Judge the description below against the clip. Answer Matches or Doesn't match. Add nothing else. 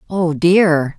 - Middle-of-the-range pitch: Matches